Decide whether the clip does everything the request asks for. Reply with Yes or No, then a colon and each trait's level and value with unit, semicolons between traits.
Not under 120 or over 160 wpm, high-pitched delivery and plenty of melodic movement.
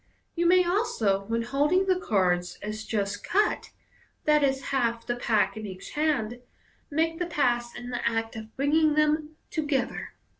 Yes: average, 155 wpm; very high, 260 Hz; wide, 5.8 semitones